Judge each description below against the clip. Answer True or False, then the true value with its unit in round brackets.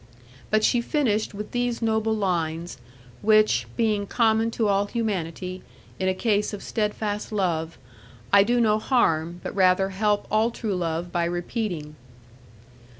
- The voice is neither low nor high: False (205 Hz)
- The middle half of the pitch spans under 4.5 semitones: True (3.5 semitones)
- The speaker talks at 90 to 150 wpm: True (145 wpm)